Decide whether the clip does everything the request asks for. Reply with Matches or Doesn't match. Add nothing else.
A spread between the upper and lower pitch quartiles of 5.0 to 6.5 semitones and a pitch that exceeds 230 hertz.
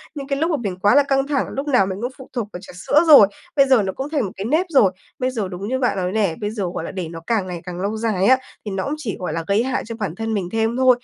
Doesn't match